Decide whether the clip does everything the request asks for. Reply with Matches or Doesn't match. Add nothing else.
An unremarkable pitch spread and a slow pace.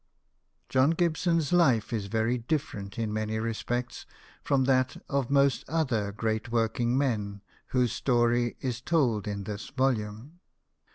Matches